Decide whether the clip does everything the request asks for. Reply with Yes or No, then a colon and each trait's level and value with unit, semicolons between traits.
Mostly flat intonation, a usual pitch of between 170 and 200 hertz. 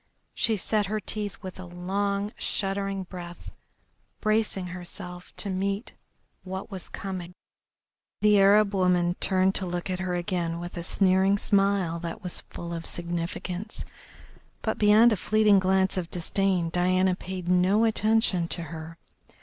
Yes: narrow, 2.2 semitones; medium, 185 Hz